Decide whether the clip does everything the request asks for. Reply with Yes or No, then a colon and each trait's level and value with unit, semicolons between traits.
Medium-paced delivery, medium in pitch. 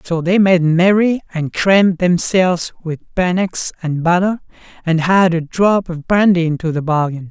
Yes: average, 165 wpm; medium, 175 Hz